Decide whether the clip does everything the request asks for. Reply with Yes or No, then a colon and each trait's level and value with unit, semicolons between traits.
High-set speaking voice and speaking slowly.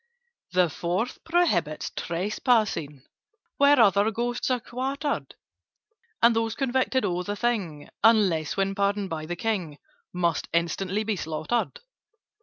Yes: high, 205 Hz; slow, 120 wpm